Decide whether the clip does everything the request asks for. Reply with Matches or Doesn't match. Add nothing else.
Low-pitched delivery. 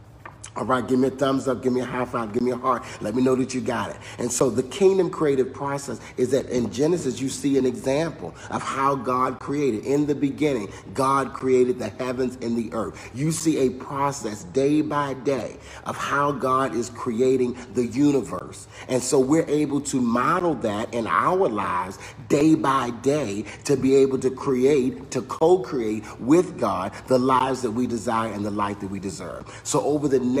Matches